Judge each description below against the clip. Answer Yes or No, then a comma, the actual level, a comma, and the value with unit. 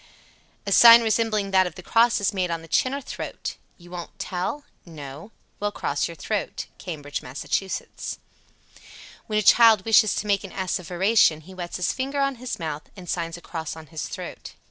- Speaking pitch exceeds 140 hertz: Yes, high, 190 Hz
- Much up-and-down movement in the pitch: No, average, 4.6 semitones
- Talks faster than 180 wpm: Yes, average, 195 wpm